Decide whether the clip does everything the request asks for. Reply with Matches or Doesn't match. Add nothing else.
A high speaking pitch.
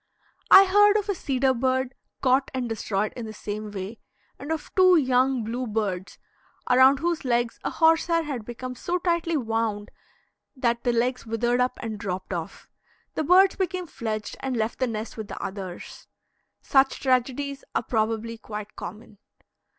Matches